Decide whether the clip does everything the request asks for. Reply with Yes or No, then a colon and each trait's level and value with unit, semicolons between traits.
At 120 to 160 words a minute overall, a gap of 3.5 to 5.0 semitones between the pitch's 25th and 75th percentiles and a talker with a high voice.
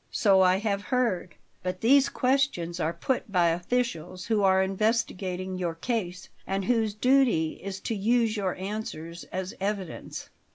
Yes: average, 150 wpm; average, 3.8 semitones; high, 195 Hz